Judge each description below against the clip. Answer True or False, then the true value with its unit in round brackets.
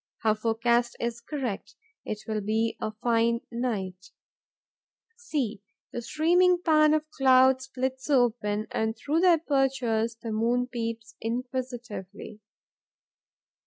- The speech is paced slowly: True (120 wpm)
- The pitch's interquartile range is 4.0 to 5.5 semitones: False (3.3 semitones)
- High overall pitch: True (240 Hz)